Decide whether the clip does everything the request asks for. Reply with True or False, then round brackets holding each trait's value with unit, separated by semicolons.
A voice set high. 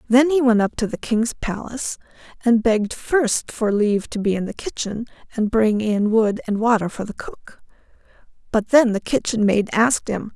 True (220 Hz)